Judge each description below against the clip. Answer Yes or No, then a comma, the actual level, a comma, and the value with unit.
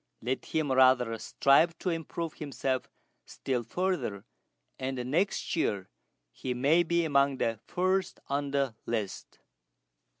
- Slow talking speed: Yes, slow, 125 wpm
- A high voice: No, medium, 140 Hz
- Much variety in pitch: No, average, 4.8 semitones